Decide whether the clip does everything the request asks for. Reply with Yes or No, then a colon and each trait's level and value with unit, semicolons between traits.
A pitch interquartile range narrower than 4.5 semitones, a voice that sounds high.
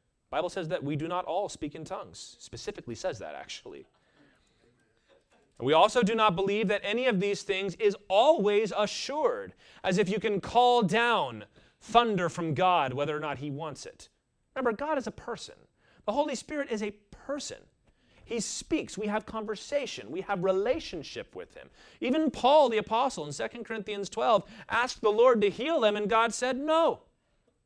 Yes: average, 3.9 semitones; high, 215 Hz